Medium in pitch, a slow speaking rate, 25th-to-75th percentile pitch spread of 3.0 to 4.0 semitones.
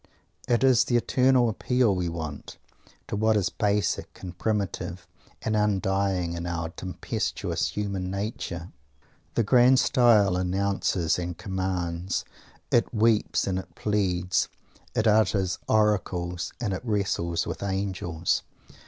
No: very low, 95 Hz; slow, 125 wpm; average, 3.4 semitones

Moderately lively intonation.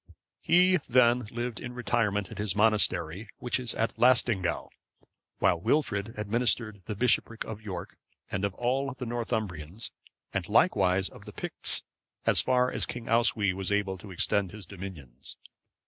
Yes: average, 3.9 semitones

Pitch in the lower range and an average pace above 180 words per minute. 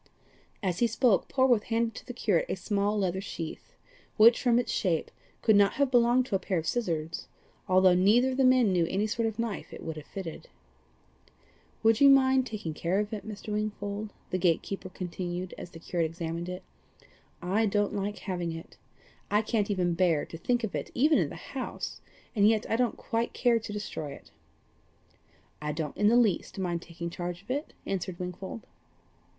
No: high, 200 Hz; average, 195 wpm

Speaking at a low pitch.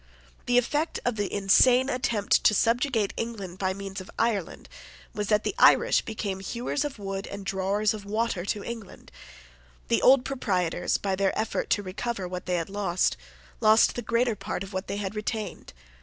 No: high, 205 Hz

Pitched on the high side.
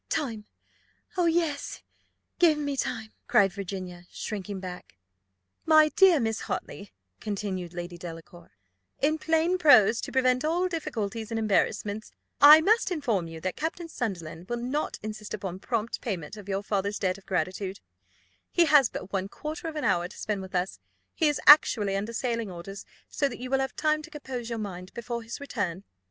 Yes: high, 220 Hz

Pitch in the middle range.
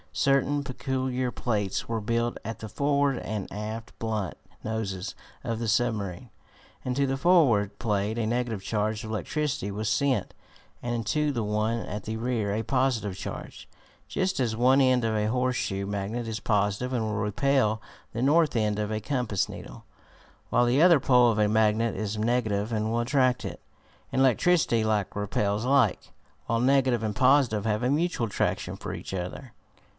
No: low, 115 Hz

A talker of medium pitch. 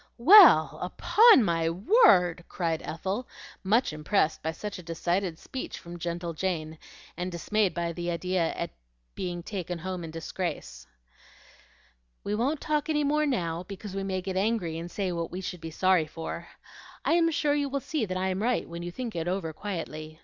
Yes: medium, 180 Hz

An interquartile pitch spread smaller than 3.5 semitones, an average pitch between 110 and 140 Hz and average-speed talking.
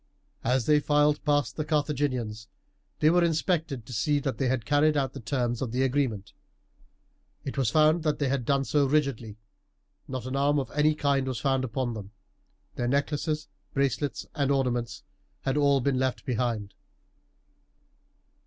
Yes: average, 2.8 semitones; low, 135 Hz; average, 165 wpm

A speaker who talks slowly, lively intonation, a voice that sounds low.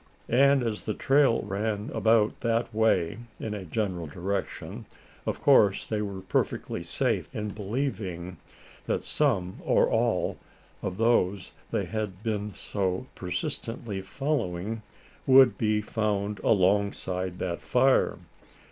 No: slow, 120 wpm; average, 3.2 semitones; low, 105 Hz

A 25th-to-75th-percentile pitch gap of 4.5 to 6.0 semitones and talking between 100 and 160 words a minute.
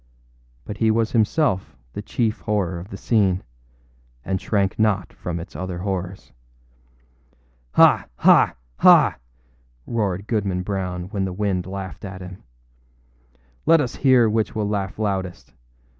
No: average, 2.7 semitones; slow, 135 wpm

